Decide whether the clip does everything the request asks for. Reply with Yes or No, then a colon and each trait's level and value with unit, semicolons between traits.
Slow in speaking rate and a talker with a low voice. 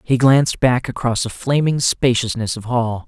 No: average, 175 wpm; low, 120 Hz